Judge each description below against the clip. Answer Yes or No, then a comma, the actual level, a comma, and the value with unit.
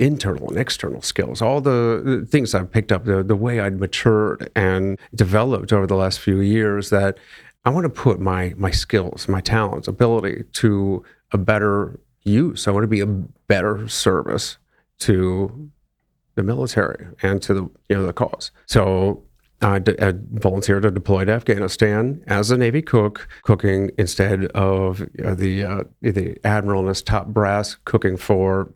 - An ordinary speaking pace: Yes, average, 165 wpm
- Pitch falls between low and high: No, low, 100 Hz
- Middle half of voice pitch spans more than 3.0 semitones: No, narrow, 2.4 semitones